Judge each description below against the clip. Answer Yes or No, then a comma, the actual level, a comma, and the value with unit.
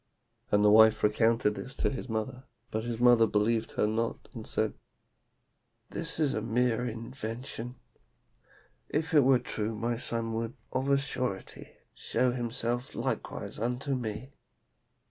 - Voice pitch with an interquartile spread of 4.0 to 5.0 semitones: No, narrow, 2.5 semitones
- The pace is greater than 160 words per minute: No, average, 145 wpm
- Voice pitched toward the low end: Yes, low, 115 Hz